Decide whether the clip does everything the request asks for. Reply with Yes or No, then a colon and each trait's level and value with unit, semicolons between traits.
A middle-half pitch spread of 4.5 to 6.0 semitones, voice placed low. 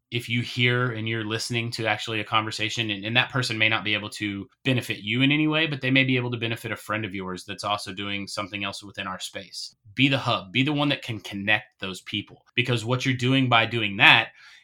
No: average, 3.2 semitones; low, 110 Hz